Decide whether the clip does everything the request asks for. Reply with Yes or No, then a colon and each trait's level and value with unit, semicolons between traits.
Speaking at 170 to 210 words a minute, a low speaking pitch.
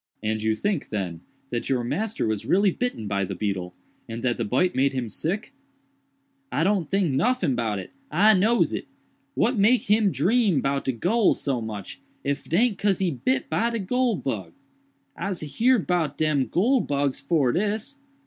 No: average, 180 wpm; medium, 155 Hz